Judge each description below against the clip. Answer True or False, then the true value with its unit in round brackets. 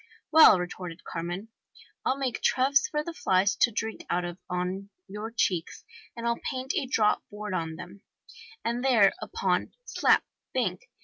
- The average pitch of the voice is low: False (210 Hz)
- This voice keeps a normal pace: True (160 wpm)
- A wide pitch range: True (6.1 semitones)